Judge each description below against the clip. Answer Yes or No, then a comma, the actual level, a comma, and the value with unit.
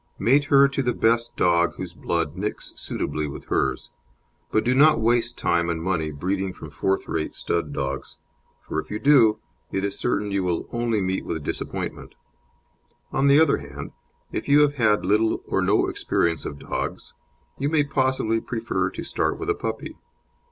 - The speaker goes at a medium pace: Yes, average, 180 wpm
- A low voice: Yes, low, 105 Hz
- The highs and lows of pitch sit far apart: Yes, wide, 6.3 semitones